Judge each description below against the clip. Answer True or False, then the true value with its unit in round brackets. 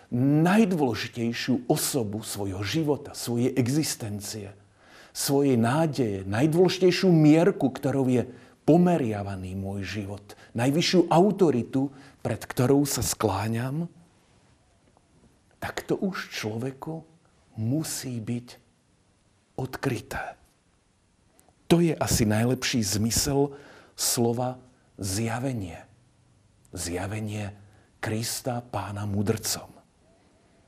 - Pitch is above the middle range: False (120 Hz)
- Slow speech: True (75 wpm)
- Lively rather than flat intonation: False (4.9 semitones)